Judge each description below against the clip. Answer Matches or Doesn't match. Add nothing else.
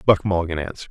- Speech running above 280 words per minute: Doesn't match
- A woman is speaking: Doesn't match